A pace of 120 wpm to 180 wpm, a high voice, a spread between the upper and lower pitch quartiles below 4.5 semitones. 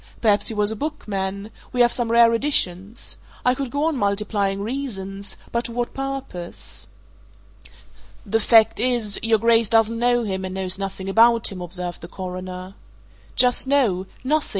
Yes: average, 160 wpm; high, 220 Hz; average, 3.9 semitones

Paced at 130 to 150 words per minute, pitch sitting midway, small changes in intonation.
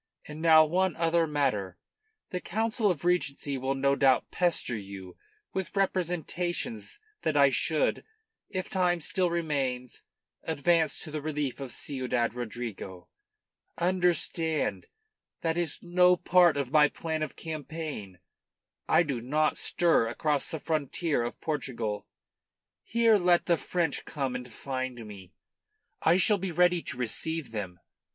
No: average, 140 wpm; medium, 155 Hz; average, 5.3 semitones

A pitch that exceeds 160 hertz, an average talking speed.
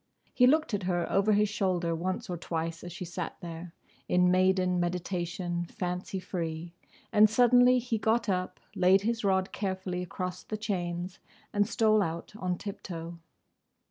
Yes: medium, 185 Hz; average, 160 wpm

